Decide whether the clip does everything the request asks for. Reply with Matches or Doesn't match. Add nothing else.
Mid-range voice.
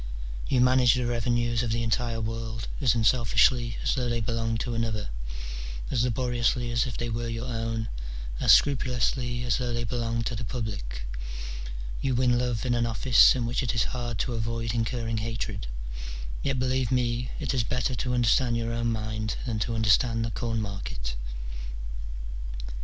Doesn't match